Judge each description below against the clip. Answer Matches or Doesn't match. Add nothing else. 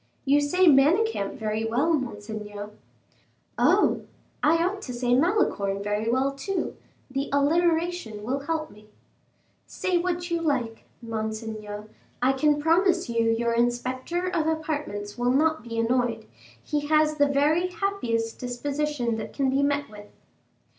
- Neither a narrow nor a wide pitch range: Doesn't match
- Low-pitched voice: Doesn't match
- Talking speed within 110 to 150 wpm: Matches